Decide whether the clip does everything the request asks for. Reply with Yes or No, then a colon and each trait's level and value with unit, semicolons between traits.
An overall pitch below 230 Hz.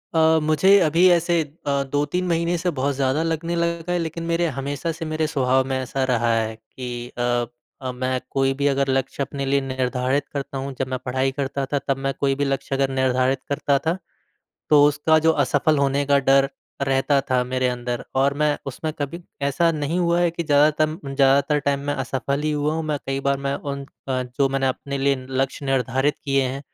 Yes: medium, 140 Hz